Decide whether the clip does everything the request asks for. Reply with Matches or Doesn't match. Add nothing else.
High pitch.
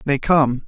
Doesn't match